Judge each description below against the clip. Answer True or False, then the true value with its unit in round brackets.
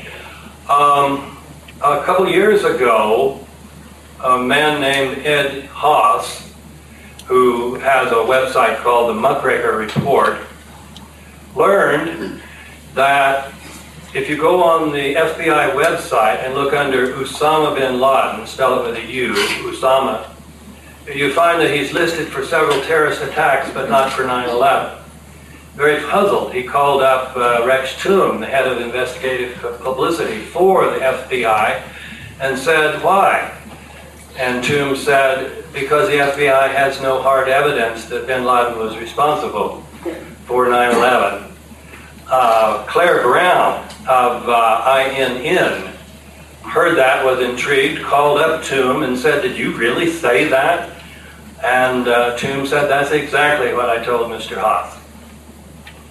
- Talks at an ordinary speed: False (125 wpm)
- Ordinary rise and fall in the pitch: False (6.6 semitones)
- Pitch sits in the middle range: False (130 Hz)